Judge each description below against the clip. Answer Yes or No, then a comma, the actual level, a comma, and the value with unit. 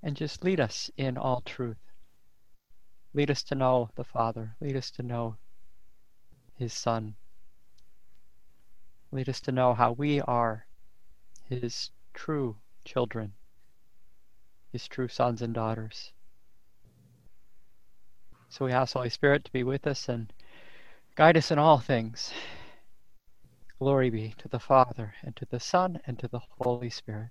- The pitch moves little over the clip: No, average, 3.4 semitones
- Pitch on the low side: Yes, low, 125 Hz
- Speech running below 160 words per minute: Yes, average, 140 wpm